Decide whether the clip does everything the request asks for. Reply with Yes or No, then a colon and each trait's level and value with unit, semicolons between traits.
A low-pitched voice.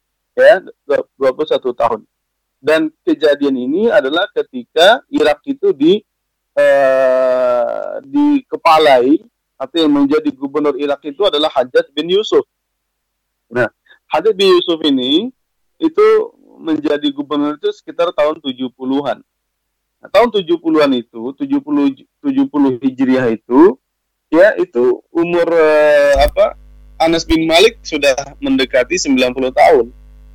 No: medium, 170 Hz